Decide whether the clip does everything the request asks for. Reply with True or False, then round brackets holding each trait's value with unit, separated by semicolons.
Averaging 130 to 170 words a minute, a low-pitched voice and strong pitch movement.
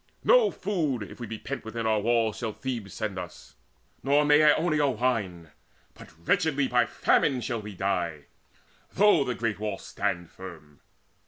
True (155 wpm; 115 Hz; 5.9 semitones)